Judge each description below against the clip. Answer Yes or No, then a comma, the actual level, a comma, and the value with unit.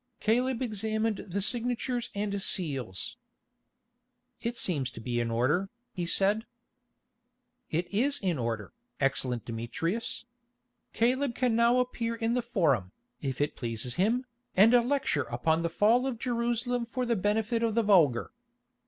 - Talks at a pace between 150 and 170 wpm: No, average, 140 wpm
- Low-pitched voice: No, high, 210 Hz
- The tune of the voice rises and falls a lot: Yes, wide, 8.4 semitones